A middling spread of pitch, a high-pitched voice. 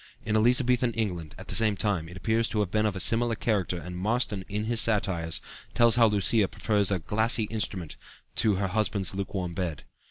No: average, 3.3 semitones; low, 105 Hz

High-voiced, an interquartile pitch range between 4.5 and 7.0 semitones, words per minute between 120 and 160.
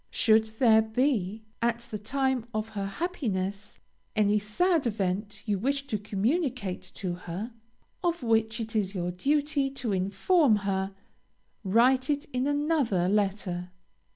Yes: high, 220 Hz; average, 5.2 semitones; slow, 135 wpm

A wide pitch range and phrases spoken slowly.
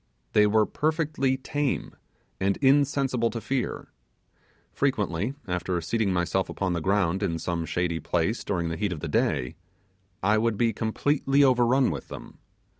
No: wide, 7.0 semitones; average, 150 wpm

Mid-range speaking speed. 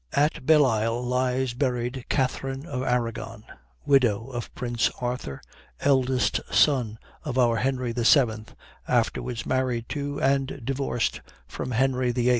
No: slow, 120 wpm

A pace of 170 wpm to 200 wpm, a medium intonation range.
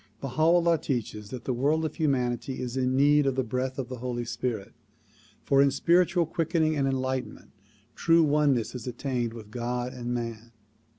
Yes: average, 175 wpm; average, 3.5 semitones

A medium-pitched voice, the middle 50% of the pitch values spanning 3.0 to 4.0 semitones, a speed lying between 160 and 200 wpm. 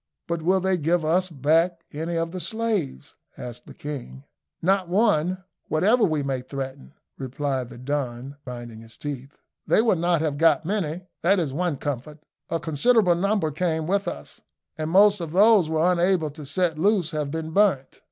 No: medium, 160 Hz; average, 4.4 semitones; average, 180 wpm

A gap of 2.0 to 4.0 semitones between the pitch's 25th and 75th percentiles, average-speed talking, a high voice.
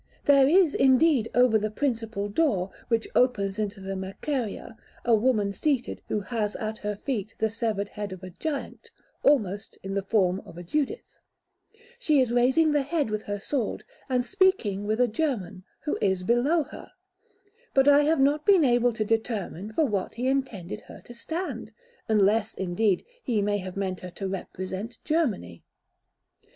No: average, 5.2 semitones; average, 170 wpm; high, 225 Hz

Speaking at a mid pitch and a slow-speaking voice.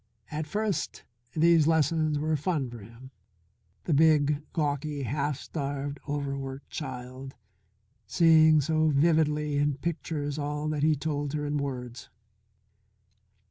Yes: medium, 145 Hz; slow, 120 wpm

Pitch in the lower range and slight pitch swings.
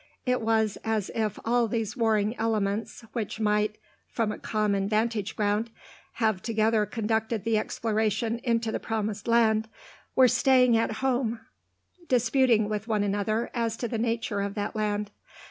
No: high, 220 Hz; narrow, 1.5 semitones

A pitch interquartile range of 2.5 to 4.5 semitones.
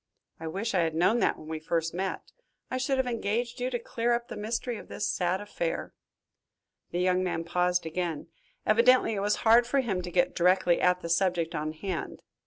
No: average, 5.1 semitones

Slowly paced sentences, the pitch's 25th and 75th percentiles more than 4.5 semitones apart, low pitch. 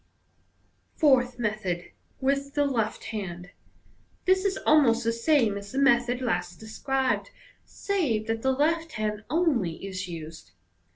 No: slow, 130 wpm; average, 5.1 semitones; high, 240 Hz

